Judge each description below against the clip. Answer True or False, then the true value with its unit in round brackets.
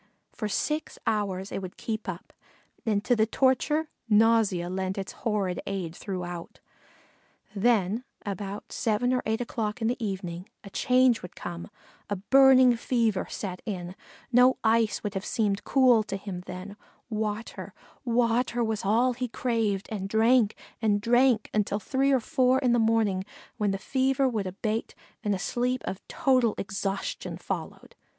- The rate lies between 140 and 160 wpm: True (155 wpm)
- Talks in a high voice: True (220 Hz)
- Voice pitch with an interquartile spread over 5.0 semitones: False (3.8 semitones)